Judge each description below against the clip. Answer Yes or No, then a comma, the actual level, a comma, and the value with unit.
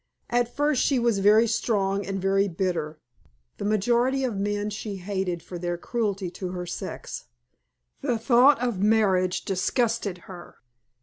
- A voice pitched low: No, high, 200 Hz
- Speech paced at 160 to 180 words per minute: No, average, 145 wpm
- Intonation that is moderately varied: Yes, average, 4.0 semitones